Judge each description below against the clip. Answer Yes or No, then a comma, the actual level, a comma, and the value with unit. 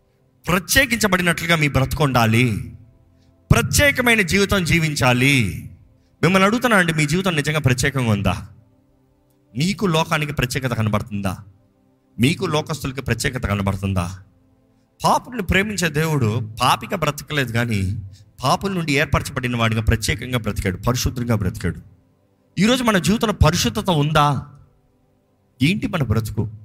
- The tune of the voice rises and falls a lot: Yes, wide, 6.6 semitones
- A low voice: Yes, low, 130 Hz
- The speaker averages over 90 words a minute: Yes, average, 100 wpm